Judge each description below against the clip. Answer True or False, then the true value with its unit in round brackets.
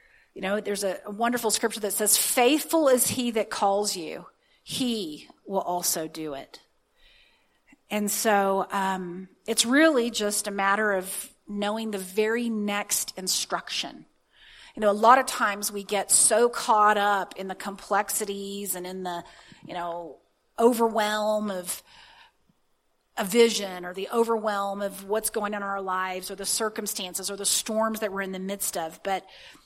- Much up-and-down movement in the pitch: False (2.4 semitones)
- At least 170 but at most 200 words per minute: False (160 wpm)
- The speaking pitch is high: True (205 Hz)